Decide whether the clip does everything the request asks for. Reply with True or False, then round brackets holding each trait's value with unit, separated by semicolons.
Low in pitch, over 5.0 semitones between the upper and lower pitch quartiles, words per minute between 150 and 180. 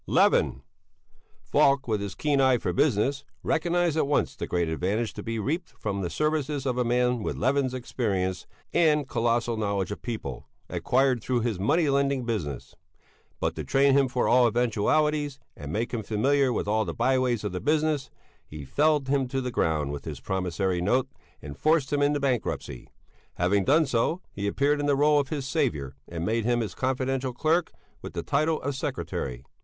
False (125 Hz; 5.5 semitones; 190 wpm)